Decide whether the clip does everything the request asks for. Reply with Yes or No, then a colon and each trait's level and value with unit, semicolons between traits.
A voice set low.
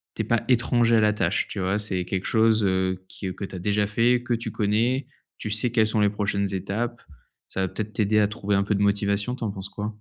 Yes: low, 105 Hz